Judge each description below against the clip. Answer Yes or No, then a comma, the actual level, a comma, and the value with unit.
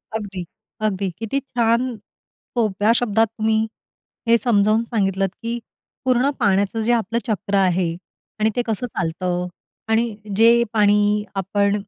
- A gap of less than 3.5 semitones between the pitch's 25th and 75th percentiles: Yes, average, 2.7 semitones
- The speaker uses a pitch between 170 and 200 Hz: No, high, 215 Hz